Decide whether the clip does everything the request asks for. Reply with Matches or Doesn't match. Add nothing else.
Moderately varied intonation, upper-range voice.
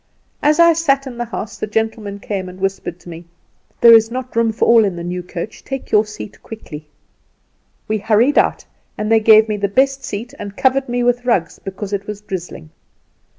Matches